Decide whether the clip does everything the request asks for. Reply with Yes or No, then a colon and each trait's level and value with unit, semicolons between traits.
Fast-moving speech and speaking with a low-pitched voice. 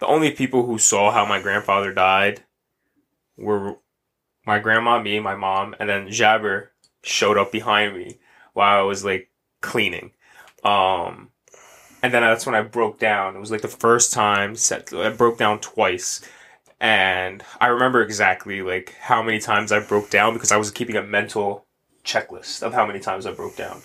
No: average, 180 wpm; low, 105 Hz